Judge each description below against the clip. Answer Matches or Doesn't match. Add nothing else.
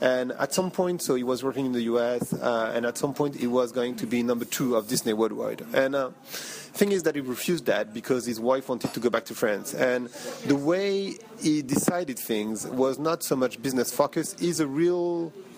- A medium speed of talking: Doesn't match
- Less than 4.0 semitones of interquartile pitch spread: Doesn't match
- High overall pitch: Doesn't match